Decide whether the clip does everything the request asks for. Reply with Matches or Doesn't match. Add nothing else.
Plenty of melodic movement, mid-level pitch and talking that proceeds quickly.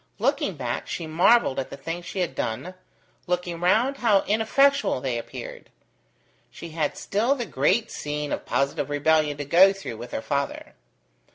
Doesn't match